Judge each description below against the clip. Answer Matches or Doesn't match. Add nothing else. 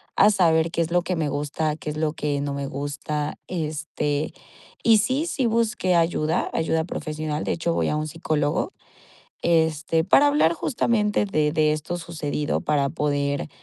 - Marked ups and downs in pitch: Doesn't match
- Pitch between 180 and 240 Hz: Doesn't match